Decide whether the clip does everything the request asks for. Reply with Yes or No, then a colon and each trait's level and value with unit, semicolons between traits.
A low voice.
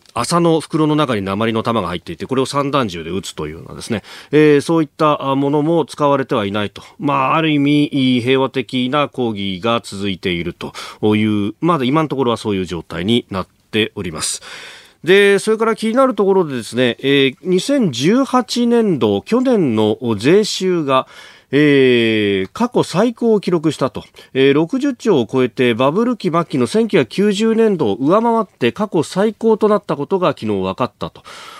No: medium, 145 Hz